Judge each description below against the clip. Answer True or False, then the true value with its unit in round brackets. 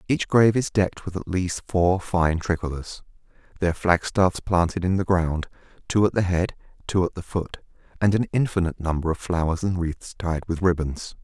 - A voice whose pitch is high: False (90 Hz)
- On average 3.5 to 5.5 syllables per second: True (5.1 syllables/s)